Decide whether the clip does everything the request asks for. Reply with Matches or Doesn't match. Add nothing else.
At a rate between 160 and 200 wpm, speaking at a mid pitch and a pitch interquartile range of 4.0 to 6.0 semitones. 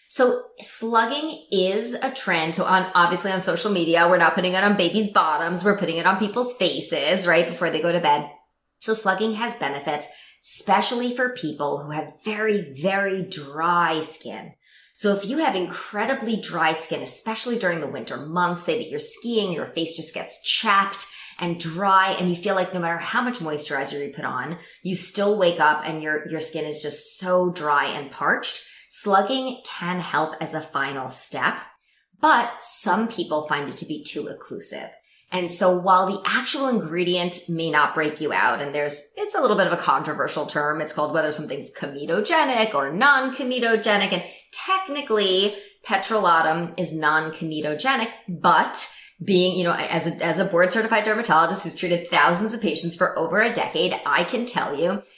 Matches